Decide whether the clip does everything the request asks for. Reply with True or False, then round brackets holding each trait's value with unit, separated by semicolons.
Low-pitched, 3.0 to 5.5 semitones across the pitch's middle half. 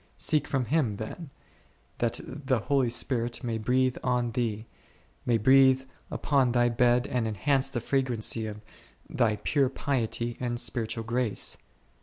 False (120 Hz; 2.5 semitones)